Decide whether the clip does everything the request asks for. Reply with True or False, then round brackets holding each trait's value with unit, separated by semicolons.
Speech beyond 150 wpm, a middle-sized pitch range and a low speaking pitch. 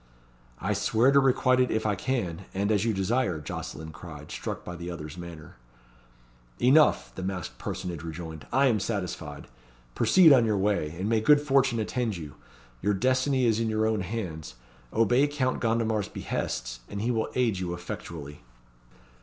False (170 wpm; 6.0 semitones; 105 Hz)